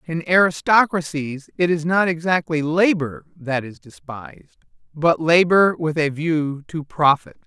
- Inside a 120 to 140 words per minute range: Yes, slow, 135 wpm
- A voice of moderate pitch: Yes, medium, 160 Hz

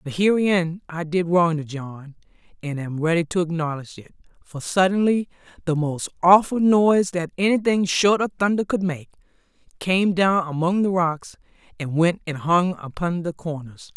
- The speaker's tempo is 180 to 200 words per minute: No, average, 165 wpm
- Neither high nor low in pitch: Yes, medium, 170 Hz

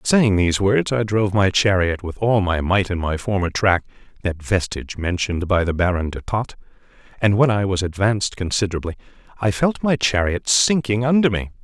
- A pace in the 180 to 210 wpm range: Yes, average, 185 wpm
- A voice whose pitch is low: Yes, low, 100 Hz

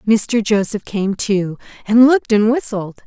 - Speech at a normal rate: Yes, average, 155 wpm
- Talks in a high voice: Yes, high, 215 Hz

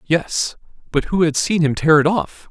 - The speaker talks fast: Yes, fast, 215 wpm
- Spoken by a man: Yes, male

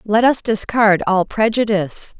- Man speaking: No, female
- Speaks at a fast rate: No, slow, 135 wpm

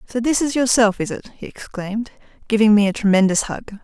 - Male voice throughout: No, female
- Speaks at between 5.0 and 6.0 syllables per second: Yes, 5.9 syllables/s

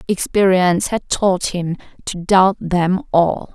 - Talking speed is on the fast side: No, slow, 135 wpm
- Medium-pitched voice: Yes, medium, 180 Hz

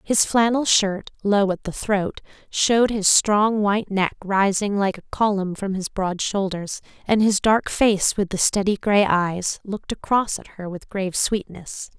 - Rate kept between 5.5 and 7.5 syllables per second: No, 4.2 syllables/s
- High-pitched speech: Yes, high, 200 Hz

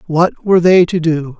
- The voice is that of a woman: No, male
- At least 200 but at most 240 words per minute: Yes, fast, 215 wpm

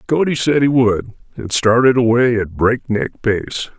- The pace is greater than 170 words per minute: No, average, 160 wpm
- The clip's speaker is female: No, male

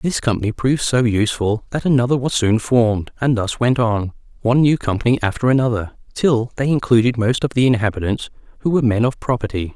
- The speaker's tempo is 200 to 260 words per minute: No, average, 190 wpm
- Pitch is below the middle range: Yes, low, 120 Hz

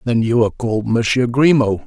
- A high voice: No, low, 120 Hz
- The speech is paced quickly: No, average, 195 wpm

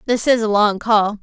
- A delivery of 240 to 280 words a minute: Yes, fast, 245 wpm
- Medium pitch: No, high, 215 Hz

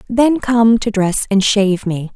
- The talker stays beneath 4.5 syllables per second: Yes, 4.3 syllables/s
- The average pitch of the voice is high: Yes, high, 215 Hz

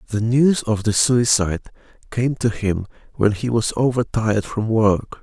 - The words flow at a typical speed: Yes, average, 160 wpm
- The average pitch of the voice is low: Yes, low, 110 Hz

